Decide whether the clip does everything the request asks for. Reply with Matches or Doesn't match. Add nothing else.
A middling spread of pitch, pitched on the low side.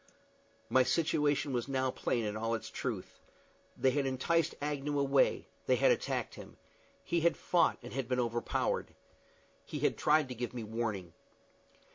Matches